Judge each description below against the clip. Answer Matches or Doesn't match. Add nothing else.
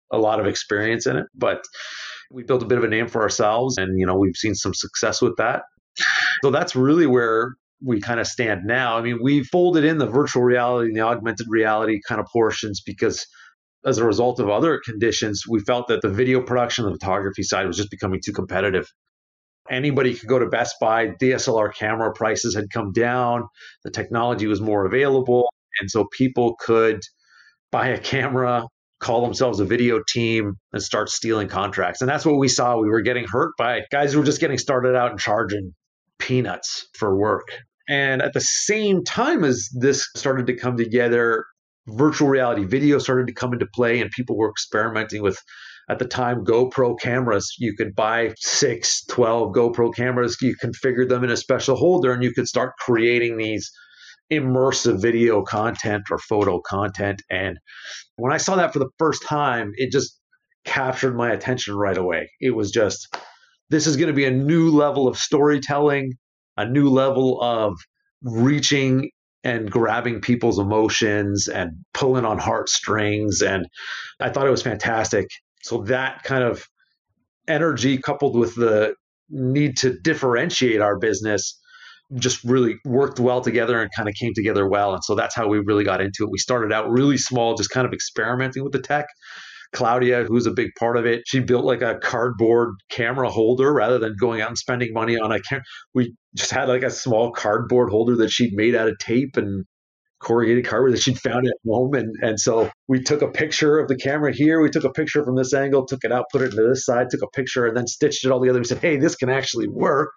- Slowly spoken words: Doesn't match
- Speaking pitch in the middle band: Doesn't match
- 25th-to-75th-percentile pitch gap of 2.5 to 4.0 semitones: Matches